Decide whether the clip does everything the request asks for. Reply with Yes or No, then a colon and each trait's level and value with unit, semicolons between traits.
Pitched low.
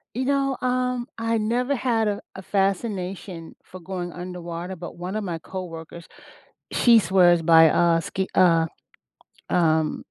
No: medium, 185 Hz